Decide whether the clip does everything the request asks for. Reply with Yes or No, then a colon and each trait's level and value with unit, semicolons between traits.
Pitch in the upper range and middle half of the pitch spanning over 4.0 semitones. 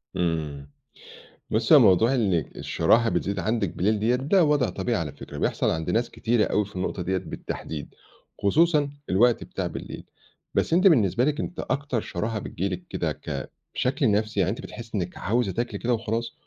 No: low, 110 Hz; average, 4.9 semitones